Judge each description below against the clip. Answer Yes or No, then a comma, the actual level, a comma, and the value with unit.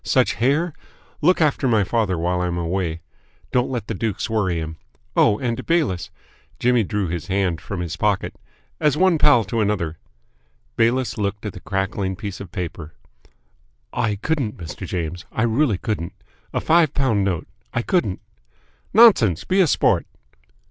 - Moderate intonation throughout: No, wide, 5.8 semitones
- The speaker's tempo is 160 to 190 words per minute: Yes, average, 165 wpm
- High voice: No, low, 105 Hz